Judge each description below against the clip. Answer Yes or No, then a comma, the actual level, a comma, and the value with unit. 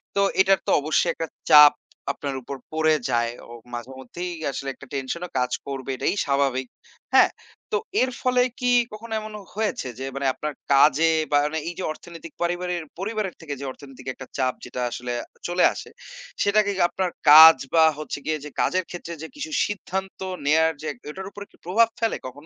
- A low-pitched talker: No, medium, 160 Hz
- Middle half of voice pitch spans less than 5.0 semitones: No, wide, 5.6 semitones